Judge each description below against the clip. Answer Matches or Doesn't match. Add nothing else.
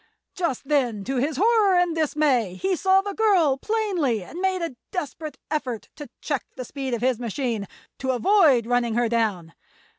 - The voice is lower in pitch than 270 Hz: Doesn't match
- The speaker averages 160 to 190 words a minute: Matches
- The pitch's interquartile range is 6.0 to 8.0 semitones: Matches